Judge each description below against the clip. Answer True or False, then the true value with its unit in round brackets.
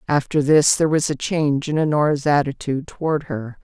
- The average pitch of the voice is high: False (145 Hz)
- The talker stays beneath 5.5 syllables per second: False (5.8 syllables/s)